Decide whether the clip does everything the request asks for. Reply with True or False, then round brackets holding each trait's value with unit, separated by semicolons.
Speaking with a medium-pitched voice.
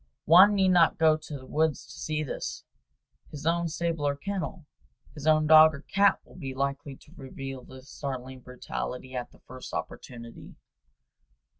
True (150 Hz)